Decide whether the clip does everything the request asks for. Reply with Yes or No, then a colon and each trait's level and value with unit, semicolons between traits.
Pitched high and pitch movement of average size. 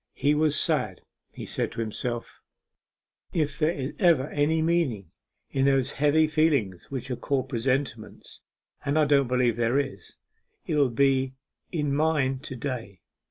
No: medium, 140 Hz; average, 3.1 semitones